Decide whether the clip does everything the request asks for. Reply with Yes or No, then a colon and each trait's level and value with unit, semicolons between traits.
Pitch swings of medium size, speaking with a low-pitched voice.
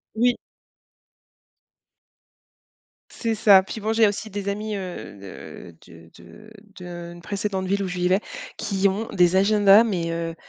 No: average, 3.1 semitones; high, 195 Hz